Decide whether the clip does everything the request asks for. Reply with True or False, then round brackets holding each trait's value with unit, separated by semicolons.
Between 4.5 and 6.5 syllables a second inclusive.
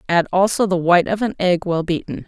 True (5.9 syllables/s)